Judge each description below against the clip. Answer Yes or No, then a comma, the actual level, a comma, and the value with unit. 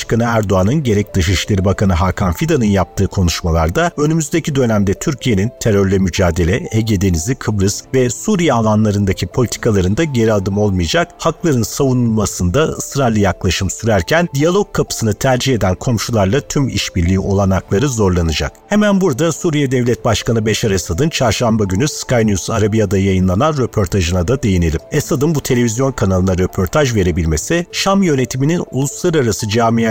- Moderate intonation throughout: No, wide, 6.0 semitones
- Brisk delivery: No, average, 125 wpm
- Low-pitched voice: Yes, low, 110 Hz